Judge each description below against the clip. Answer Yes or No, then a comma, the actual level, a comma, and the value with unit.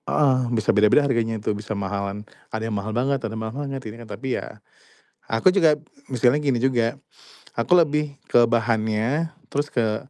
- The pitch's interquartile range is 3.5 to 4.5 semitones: Yes, average, 4.1 semitones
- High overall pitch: No, low, 115 Hz